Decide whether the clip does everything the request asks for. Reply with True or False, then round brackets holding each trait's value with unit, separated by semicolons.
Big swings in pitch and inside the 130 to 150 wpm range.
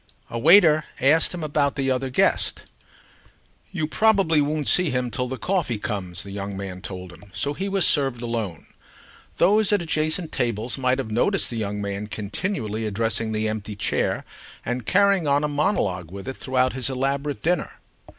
False (6.3 semitones; 175 wpm)